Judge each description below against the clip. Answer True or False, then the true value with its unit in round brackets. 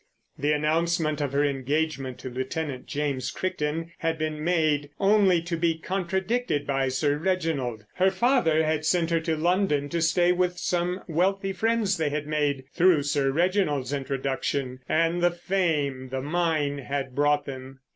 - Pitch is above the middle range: False (155 Hz)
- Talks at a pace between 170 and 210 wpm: False (155 wpm)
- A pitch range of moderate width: True (3.7 semitones)